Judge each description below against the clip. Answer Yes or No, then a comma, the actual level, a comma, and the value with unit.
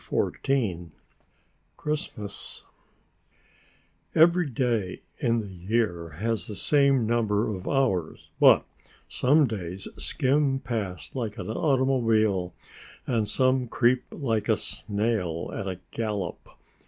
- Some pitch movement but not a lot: Yes, average, 4.9 semitones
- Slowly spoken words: Yes, slow, 110 wpm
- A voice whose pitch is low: Yes, low, 115 Hz